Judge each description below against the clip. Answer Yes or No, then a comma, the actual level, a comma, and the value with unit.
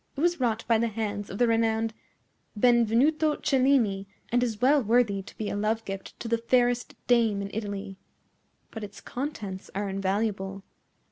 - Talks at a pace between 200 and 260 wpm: No, average, 165 wpm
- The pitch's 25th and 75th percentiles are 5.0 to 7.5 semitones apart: No, average, 3.3 semitones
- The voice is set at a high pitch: Yes, high, 225 Hz